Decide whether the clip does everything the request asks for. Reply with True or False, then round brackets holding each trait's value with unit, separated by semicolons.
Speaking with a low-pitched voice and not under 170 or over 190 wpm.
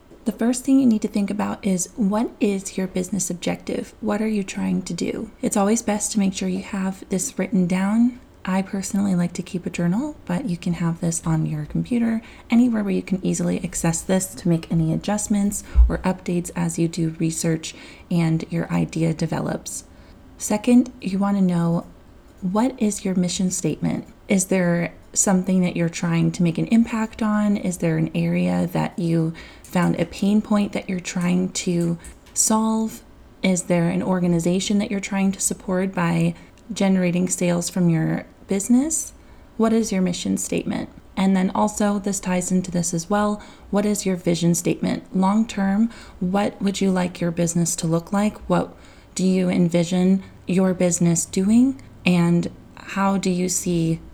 False (185 Hz; 175 wpm)